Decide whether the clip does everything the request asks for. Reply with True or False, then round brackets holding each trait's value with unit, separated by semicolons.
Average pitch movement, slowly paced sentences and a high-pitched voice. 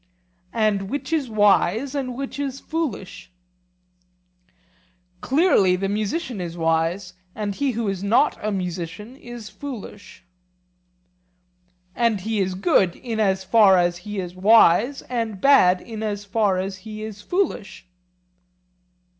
True (4.2 semitones; 130 wpm; 210 Hz)